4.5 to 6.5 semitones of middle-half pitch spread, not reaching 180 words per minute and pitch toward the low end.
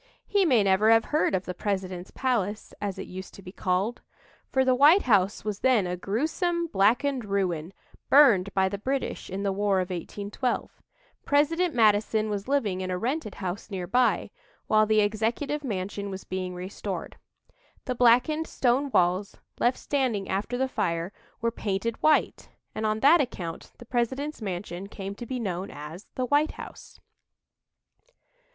No: average, 5.2 semitones; average, 160 wpm; high, 210 Hz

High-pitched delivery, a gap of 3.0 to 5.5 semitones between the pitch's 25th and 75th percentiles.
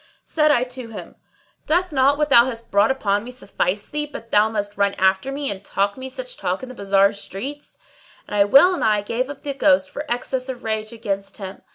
Yes: high, 230 Hz; average, 5.1 semitones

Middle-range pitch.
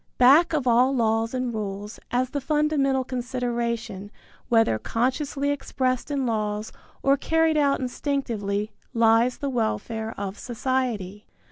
No: high, 245 Hz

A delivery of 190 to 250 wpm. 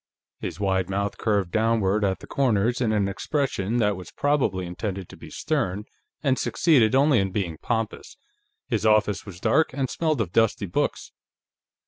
No: average, 165 wpm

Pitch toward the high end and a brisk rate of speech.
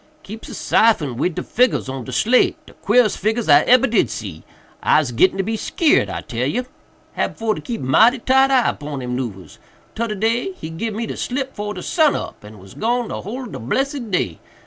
Yes: high, 215 Hz; fast, 215 wpm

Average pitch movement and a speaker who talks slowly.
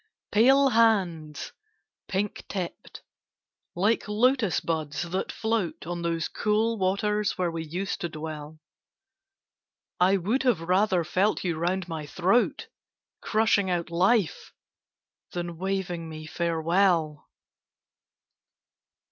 Yes: average, 4.0 semitones; slow, 105 wpm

